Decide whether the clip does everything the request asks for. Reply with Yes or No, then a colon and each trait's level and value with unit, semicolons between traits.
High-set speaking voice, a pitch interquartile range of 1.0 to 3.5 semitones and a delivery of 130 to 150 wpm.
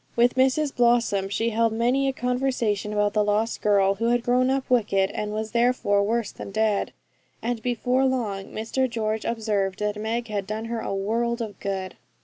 No: high, 225 Hz; average, 2.7 semitones; average, 185 wpm